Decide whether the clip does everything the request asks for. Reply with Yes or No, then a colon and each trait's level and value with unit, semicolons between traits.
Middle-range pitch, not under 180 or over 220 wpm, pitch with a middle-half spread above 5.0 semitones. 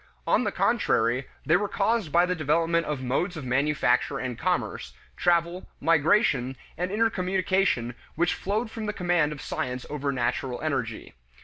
No: medium, 160 Hz; average, 150 wpm; wide, 5.6 semitones